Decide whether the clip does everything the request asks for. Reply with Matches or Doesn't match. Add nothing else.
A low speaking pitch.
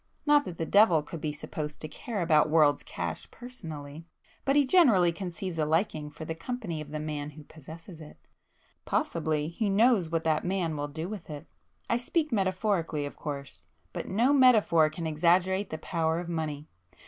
Doesn't match